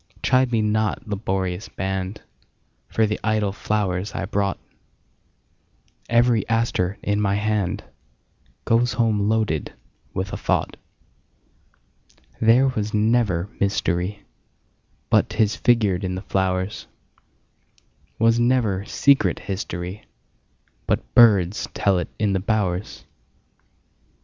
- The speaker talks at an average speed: No, slow, 90 wpm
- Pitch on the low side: Yes, low, 105 Hz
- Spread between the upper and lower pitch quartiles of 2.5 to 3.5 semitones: Yes, average, 2.9 semitones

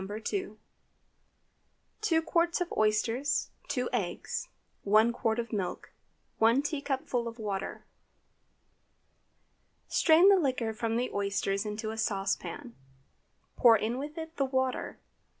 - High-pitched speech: Yes, high, 235 Hz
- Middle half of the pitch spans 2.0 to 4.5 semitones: No, average, 5.0 semitones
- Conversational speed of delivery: No, slow, 115 wpm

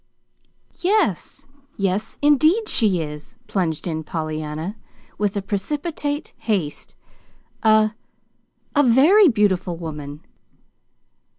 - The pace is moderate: No, slow, 85 wpm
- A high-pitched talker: Yes, high, 200 Hz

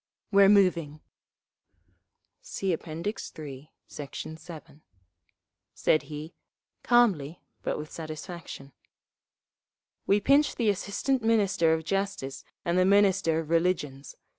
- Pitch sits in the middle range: Yes, medium, 170 Hz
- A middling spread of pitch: Yes, average, 4.4 semitones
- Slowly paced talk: Yes, slow, 105 wpm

